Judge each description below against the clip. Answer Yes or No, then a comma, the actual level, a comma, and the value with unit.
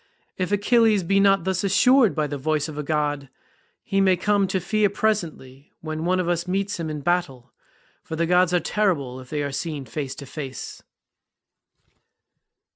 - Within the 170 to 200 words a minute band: Yes, average, 180 wpm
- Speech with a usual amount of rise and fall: Yes, average, 4.9 semitones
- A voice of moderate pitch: Yes, medium, 170 Hz